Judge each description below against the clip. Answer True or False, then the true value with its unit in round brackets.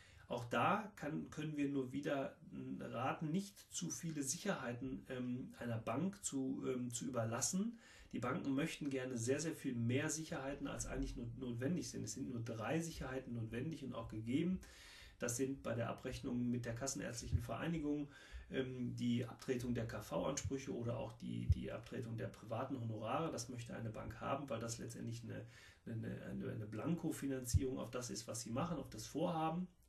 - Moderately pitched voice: False (130 Hz)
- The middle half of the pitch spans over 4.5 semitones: False (3.6 semitones)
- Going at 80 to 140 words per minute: False (170 wpm)